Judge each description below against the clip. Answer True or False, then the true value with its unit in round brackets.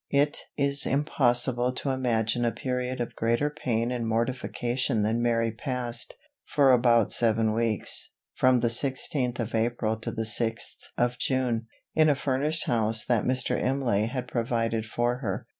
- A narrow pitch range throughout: True (2.2 semitones)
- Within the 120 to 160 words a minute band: True (155 wpm)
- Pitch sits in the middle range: False (120 Hz)